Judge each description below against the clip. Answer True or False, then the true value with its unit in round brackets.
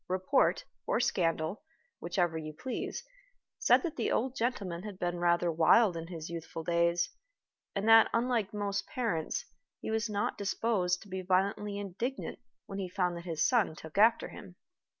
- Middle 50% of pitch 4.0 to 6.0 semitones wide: True (4.4 semitones)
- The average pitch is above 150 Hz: True (190 Hz)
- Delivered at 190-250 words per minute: False (165 wpm)